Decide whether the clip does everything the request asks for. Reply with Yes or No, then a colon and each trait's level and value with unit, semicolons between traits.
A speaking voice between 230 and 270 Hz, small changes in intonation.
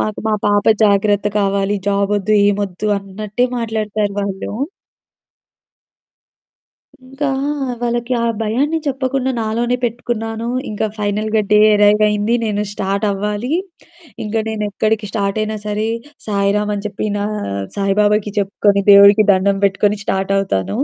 No: high, 210 Hz; narrow, 1.7 semitones